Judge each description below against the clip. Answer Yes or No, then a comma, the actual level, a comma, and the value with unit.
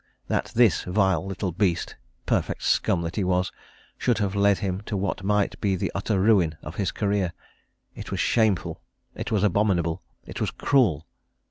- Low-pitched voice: Yes, very low, 95 Hz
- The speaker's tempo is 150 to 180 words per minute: Yes, average, 170 wpm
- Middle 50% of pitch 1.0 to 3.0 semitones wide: Yes, narrow, 2.4 semitones